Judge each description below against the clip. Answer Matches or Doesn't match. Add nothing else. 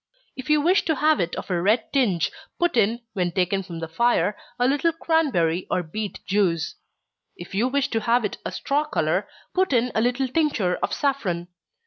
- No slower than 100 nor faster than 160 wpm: Doesn't match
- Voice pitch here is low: Doesn't match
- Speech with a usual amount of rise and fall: Doesn't match